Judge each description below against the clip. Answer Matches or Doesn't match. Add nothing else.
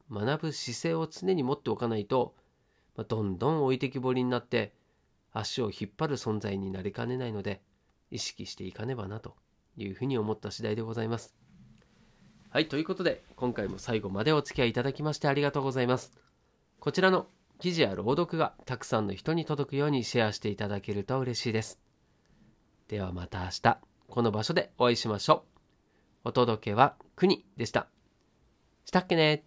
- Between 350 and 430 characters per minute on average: Matches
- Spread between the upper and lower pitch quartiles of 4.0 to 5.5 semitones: Matches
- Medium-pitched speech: Doesn't match